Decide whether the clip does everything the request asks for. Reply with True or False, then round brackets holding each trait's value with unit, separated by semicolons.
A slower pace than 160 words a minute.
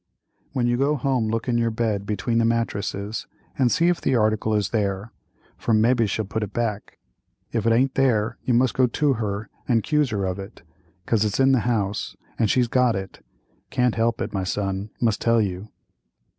False (195 wpm)